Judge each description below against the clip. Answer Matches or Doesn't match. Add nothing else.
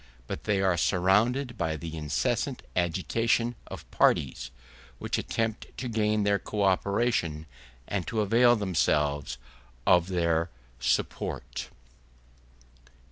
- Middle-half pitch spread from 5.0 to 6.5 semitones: Matches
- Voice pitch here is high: Doesn't match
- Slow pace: Matches